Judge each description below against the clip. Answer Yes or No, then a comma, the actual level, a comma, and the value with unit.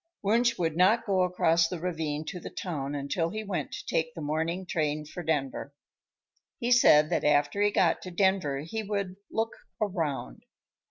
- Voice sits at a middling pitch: Yes, medium, 170 Hz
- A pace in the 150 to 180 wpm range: Yes, average, 175 wpm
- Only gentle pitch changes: No, average, 4.5 semitones